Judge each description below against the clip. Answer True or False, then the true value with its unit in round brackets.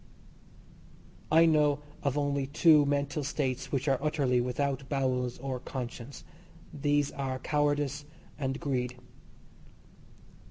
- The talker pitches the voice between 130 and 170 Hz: True (140 Hz)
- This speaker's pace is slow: True (110 wpm)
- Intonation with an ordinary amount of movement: False (1.9 semitones)